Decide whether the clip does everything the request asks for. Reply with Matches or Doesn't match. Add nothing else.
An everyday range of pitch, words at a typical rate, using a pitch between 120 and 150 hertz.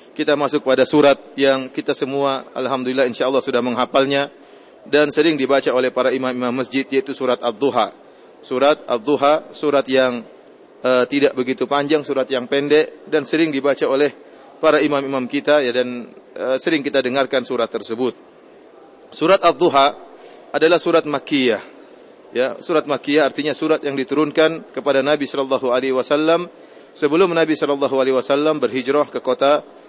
Doesn't match